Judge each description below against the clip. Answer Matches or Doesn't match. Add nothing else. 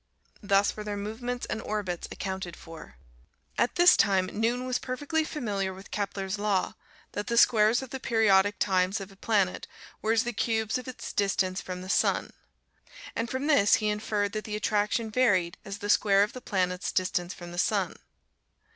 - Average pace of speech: Matches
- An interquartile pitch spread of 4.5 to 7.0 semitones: Doesn't match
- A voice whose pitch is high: Matches